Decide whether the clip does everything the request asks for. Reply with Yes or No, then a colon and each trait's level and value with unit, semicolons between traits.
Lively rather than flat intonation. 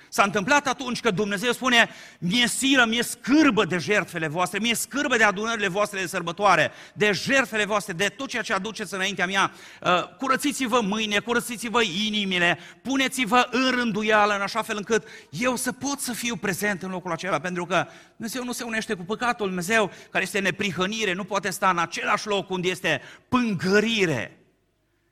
No: average, 4.0 semitones